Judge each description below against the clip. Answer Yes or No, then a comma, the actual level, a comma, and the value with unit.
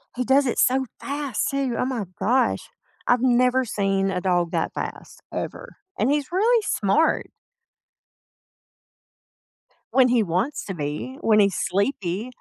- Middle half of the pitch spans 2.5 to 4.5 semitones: No, wide, 5.4 semitones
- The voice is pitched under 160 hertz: No, high, 245 Hz